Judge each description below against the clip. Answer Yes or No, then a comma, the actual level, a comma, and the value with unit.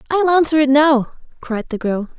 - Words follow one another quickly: No, average, 190 wpm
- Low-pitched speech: No, very high, 280 Hz